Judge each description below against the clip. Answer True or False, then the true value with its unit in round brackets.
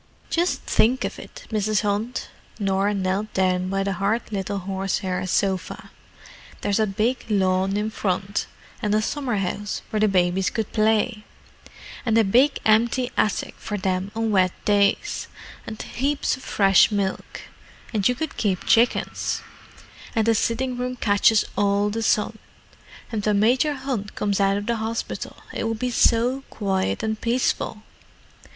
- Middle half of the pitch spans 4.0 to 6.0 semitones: False (2.7 semitones)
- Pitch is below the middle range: False (210 Hz)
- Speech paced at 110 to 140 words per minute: False (155 wpm)